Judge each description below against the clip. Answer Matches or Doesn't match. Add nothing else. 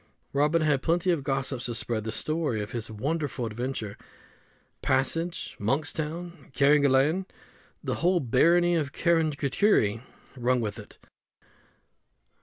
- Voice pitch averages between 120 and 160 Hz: Matches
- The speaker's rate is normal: Doesn't match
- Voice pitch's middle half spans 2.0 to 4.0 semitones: Doesn't match